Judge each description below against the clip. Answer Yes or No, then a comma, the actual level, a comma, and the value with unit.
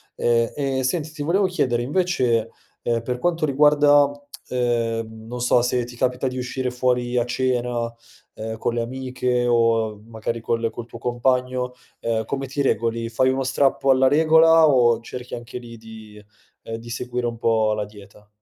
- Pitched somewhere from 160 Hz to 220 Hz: No, low, 125 Hz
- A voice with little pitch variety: Yes, narrow, 2.1 semitones